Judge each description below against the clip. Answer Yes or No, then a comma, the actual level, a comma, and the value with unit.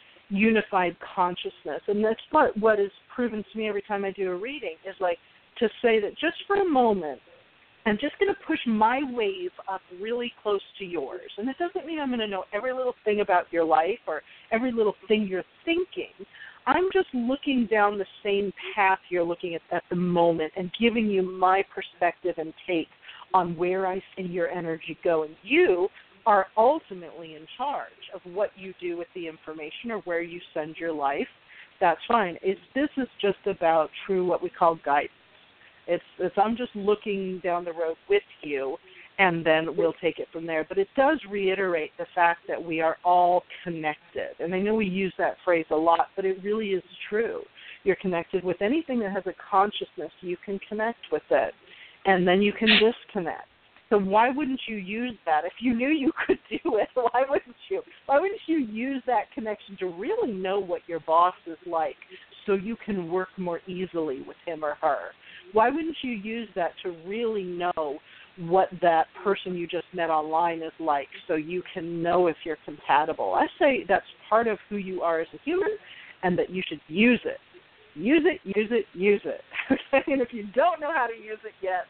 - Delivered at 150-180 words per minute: No, average, 200 wpm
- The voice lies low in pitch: No, high, 195 Hz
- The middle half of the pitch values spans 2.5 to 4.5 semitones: No, average, 4.9 semitones